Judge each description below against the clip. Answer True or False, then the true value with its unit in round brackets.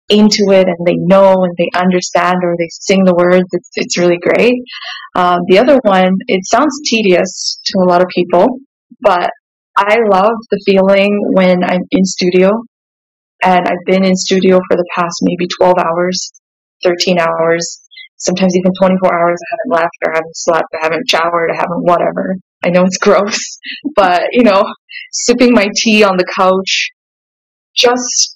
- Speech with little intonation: False (3.5 semitones)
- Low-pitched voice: False (185 Hz)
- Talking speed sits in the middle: True (175 wpm)